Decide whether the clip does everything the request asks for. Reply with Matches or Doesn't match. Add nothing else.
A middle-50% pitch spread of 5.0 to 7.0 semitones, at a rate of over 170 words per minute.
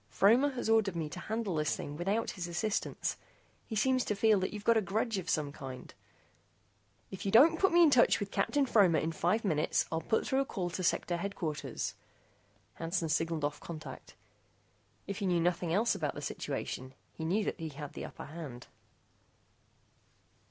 Matches